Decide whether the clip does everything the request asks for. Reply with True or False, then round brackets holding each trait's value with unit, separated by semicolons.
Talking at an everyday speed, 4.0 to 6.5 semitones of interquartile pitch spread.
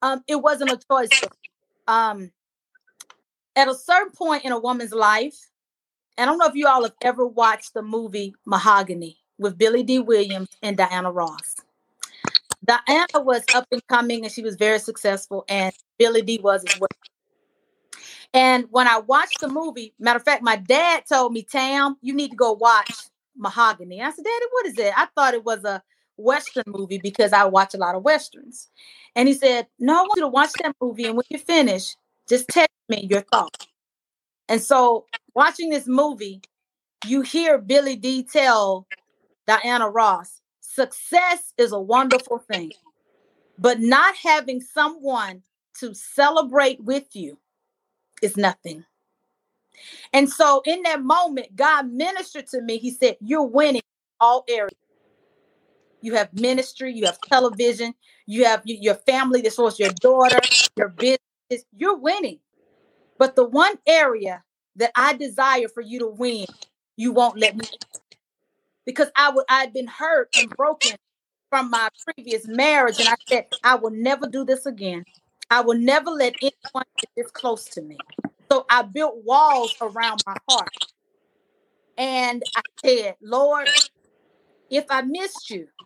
True (165 wpm; 4.3 semitones)